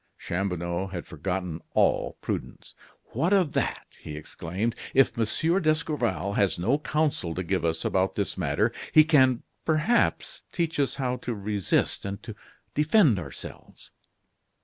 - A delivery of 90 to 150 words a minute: Yes, average, 140 wpm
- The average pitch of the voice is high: No, low, 115 Hz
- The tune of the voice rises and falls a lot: Yes, wide, 8.8 semitones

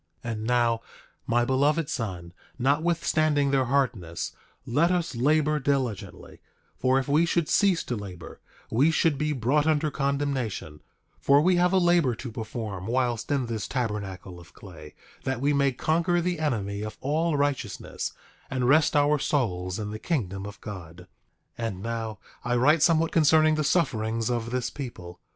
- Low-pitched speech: Yes, low, 130 Hz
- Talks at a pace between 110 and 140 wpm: No, average, 165 wpm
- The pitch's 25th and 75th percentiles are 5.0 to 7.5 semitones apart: Yes, wide, 5.6 semitones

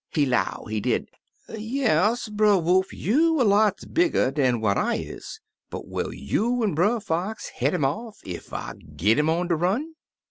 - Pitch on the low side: No, high, 190 Hz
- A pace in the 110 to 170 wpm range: No, average, 180 wpm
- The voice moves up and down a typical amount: No, wide, 7.3 semitones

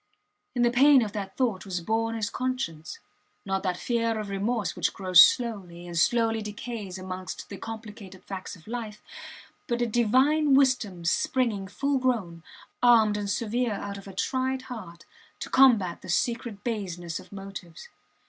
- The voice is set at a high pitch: Yes, high, 215 Hz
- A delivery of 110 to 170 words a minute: Yes, average, 160 wpm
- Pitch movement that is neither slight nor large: Yes, average, 4.1 semitones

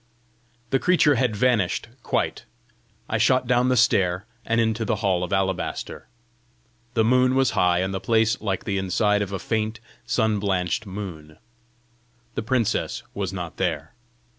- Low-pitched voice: Yes, low, 105 Hz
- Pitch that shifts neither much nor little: Yes, average, 3.8 semitones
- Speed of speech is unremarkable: Yes, average, 155 wpm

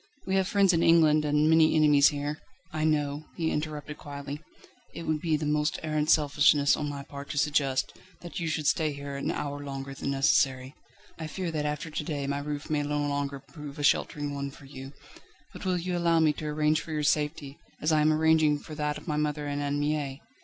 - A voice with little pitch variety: Yes, narrow, 1.6 semitones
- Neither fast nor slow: No, fast, 225 wpm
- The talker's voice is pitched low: No, medium, 150 Hz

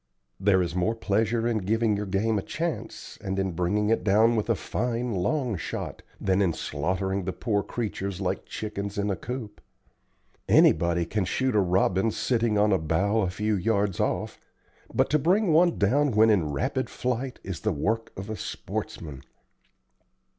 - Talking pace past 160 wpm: Yes, average, 175 wpm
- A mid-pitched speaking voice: No, low, 105 Hz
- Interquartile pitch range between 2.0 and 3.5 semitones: Yes, average, 3.2 semitones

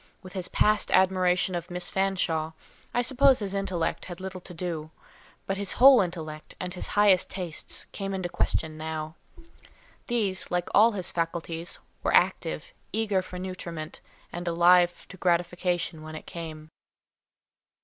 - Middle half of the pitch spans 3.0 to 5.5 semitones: No, narrow, 2.4 semitones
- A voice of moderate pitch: Yes, medium, 180 Hz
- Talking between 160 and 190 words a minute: No, average, 150 wpm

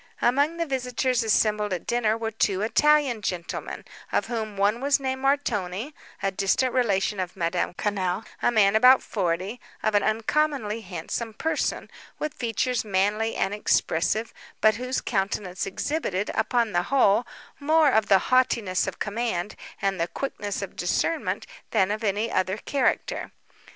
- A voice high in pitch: Yes, high, 215 Hz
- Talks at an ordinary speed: Yes, average, 150 wpm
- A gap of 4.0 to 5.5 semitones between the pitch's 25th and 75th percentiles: Yes, average, 4.3 semitones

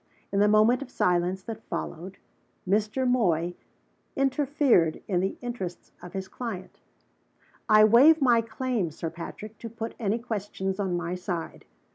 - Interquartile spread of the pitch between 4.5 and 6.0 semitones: Yes, average, 4.8 semitones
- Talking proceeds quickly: No, average, 145 wpm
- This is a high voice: Yes, high, 210 Hz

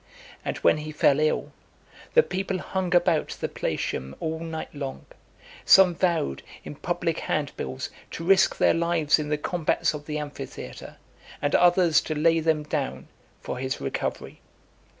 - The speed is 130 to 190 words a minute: Yes, average, 150 wpm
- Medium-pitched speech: Yes, medium, 155 Hz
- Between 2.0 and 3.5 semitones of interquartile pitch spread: Yes, average, 2.8 semitones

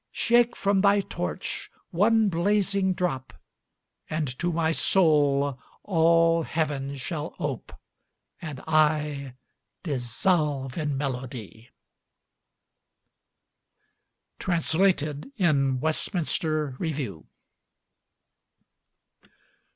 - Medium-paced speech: No, slow, 75 wpm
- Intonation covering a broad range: No, average, 4.2 semitones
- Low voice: No, medium, 155 Hz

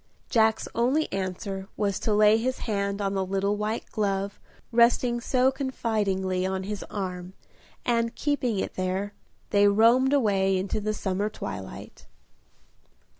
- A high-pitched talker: Yes, high, 205 Hz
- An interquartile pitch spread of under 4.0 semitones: Yes, average, 3.2 semitones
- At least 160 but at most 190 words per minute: No, slow, 135 wpm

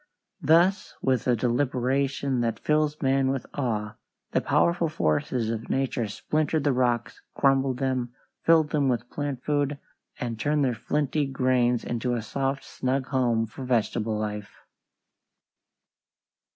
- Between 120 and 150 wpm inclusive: Yes, slow, 135 wpm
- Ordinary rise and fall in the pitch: Yes, average, 3.0 semitones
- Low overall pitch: Yes, low, 130 Hz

